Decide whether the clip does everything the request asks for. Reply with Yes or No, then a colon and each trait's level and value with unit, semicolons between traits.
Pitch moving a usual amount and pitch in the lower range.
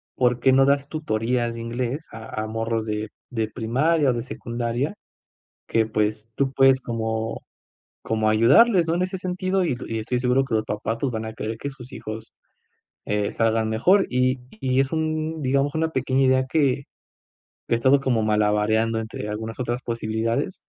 Yes: average, 3.5 semitones; low, 120 Hz